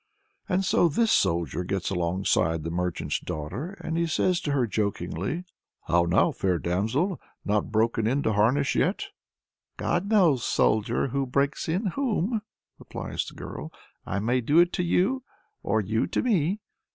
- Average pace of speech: Yes, average, 160 wpm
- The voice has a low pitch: Yes, low, 125 Hz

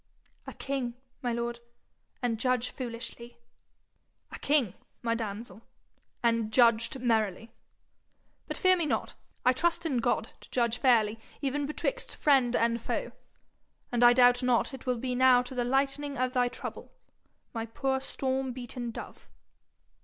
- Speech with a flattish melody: Yes, narrow, 2.2 semitones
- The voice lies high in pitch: Yes, high, 245 Hz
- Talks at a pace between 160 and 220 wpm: No, average, 145 wpm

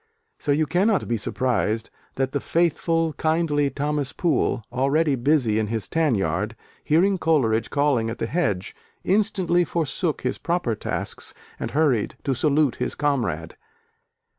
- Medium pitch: Yes, medium, 145 Hz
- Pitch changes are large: Yes, wide, 5.7 semitones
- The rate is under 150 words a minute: Yes, average, 140 wpm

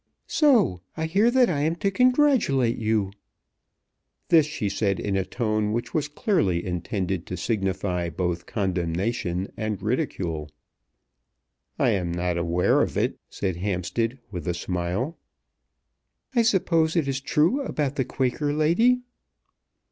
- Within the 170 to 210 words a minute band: No, slow, 135 wpm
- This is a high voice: No, low, 110 Hz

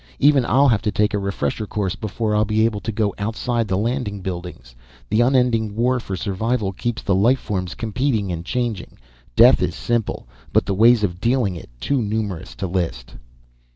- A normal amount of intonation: Yes, average, 3.7 semitones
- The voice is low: Yes, low, 105 Hz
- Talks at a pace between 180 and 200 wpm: Yes, average, 190 wpm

